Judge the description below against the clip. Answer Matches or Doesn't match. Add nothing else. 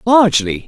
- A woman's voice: Doesn't match